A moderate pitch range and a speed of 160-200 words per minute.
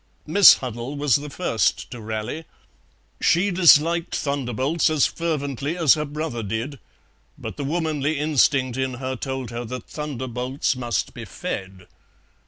No: average, 3.9 semitones; average, 140 wpm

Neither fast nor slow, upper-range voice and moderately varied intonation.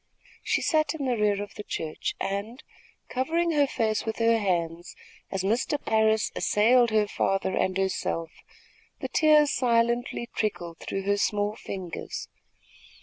Yes: average, 145 wpm; high, 215 Hz; average, 4.0 semitones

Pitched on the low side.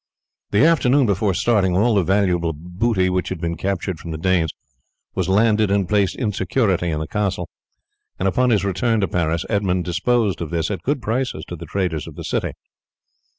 Yes: very low, 95 Hz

